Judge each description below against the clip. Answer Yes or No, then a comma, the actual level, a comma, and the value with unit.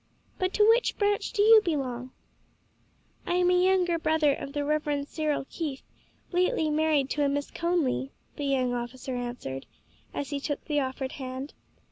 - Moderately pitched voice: No, very high, 290 Hz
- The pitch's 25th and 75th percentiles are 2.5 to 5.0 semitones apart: Yes, average, 4.7 semitones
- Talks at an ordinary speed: Yes, average, 165 wpm